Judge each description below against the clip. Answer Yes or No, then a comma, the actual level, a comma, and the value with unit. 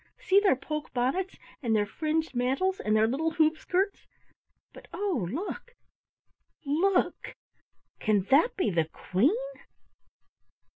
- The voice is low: No, very high, 305 Hz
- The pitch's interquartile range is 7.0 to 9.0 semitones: Yes, wide, 7.8 semitones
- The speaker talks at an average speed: No, slow, 120 wpm